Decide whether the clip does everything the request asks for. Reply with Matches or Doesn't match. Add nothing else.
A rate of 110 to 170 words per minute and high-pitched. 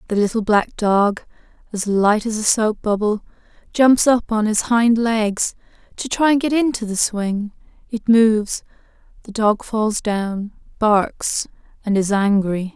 Matches